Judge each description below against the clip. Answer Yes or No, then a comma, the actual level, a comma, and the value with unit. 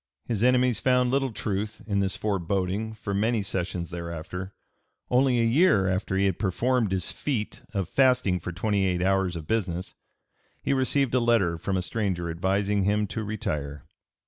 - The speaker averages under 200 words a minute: Yes, average, 170 wpm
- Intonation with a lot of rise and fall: No, average, 4.0 semitones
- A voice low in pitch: Yes, low, 100 Hz